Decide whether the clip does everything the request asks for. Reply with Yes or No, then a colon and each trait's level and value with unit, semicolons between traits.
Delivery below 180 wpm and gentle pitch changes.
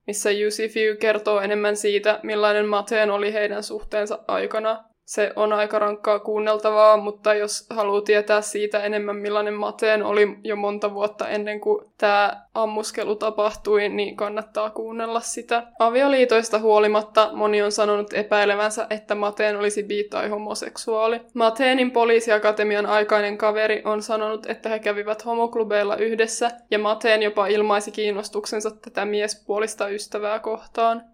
Yes: slow, 135 wpm; narrow, 1.0 semitones